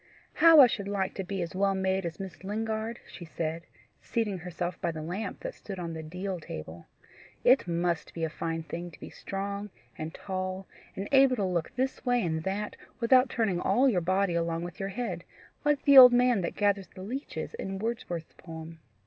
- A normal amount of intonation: Yes, average, 4.7 semitones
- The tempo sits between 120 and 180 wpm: No, average, 200 wpm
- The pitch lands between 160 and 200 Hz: Yes, high, 190 Hz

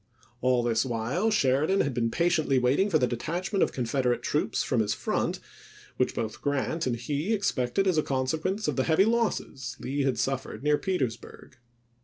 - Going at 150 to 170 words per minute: No, average, 180 wpm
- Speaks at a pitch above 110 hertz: Yes, low, 135 Hz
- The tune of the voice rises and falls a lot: Yes, wide, 5.7 semitones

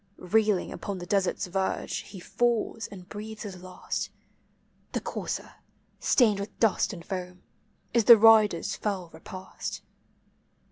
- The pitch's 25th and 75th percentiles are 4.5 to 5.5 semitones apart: No, average, 3.0 semitones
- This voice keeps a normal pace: No, slow, 130 wpm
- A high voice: Yes, high, 200 Hz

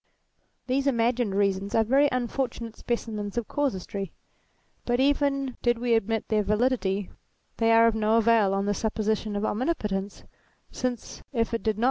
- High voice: Yes, high, 225 Hz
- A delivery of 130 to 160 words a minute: Yes, average, 155 wpm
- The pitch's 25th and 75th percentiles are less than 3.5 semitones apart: Yes, average, 3.0 semitones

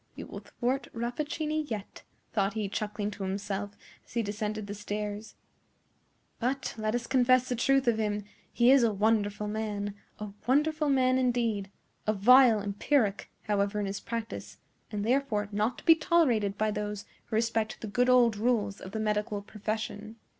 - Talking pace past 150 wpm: Yes, average, 165 wpm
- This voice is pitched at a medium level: No, high, 215 Hz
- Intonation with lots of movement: No, average, 3.2 semitones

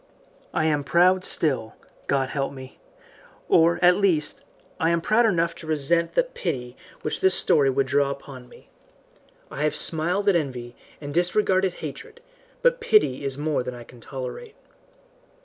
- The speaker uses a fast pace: No, average, 160 wpm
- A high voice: No, medium, 155 Hz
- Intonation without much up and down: No, average, 5.1 semitones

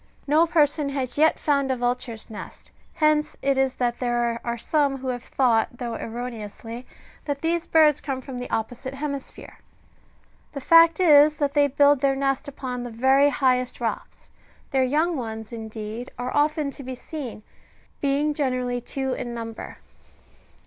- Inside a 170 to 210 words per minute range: No, average, 160 wpm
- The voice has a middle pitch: No, very high, 265 Hz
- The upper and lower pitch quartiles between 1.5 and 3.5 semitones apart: Yes, average, 3.0 semitones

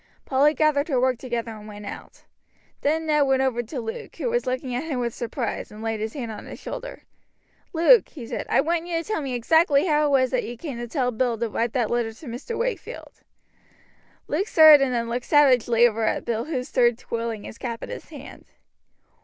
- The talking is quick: Yes, fast, 220 wpm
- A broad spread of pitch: No, average, 4.4 semitones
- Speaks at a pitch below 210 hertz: No, very high, 255 Hz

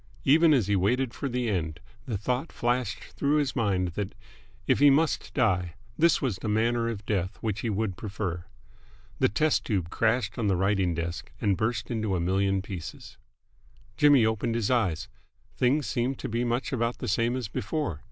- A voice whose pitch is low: Yes, low, 110 Hz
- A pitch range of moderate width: Yes, average, 4.5 semitones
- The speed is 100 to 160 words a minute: No, average, 185 wpm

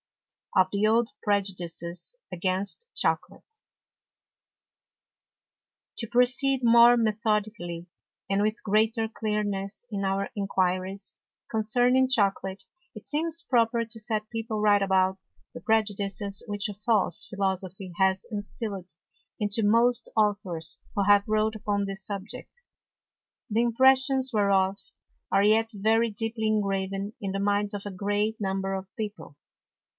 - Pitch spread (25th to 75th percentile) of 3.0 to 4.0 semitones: No, narrow, 2.4 semitones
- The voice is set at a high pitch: Yes, high, 205 Hz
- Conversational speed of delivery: No, slow, 120 wpm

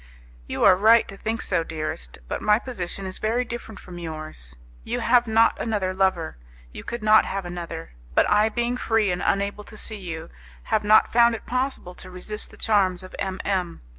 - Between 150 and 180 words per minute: No, average, 195 wpm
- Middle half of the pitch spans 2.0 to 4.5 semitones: Yes, average, 3.8 semitones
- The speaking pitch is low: No, high, 200 Hz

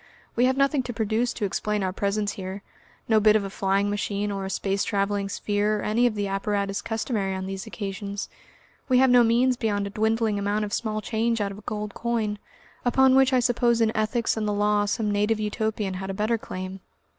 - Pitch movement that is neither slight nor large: No, narrow, 2.3 semitones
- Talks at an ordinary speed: No, fast, 215 wpm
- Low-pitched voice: No, high, 210 Hz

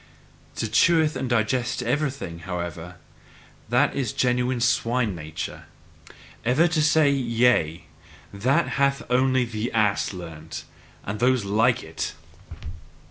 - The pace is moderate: No, slow, 125 wpm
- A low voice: Yes, low, 120 Hz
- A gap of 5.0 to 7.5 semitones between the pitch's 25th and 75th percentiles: Yes, wide, 5.4 semitones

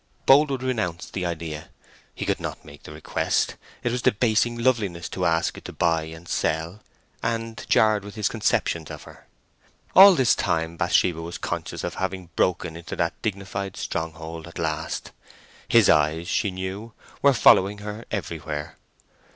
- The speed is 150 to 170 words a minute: Yes, average, 160 wpm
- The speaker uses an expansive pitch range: No, average, 5.0 semitones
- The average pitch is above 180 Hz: No, very low, 90 Hz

